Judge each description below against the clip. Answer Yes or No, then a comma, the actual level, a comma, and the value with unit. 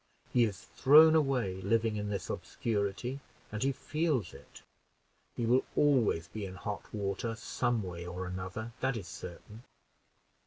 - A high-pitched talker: No, low, 110 Hz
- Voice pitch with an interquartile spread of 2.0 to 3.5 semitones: No, average, 4.7 semitones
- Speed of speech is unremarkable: Yes, average, 150 wpm